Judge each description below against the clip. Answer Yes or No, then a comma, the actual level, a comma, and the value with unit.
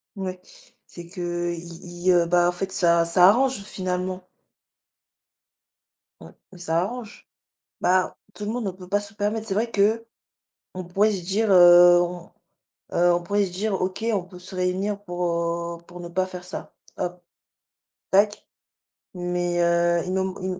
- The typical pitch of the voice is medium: Yes, medium, 180 Hz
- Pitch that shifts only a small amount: Yes, narrow, 2.3 semitones